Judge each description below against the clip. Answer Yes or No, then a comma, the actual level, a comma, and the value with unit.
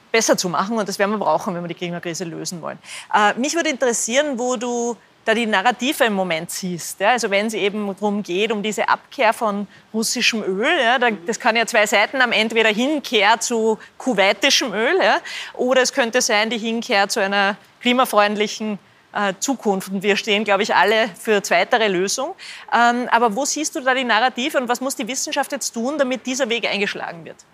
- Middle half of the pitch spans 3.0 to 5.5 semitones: Yes, average, 3.7 semitones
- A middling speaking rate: No, fast, 205 wpm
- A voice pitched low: No, high, 225 Hz